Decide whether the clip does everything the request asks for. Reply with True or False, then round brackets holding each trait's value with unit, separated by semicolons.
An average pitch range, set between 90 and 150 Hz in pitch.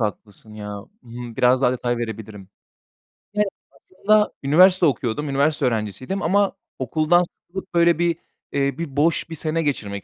False (6.7 semitones; 140 Hz)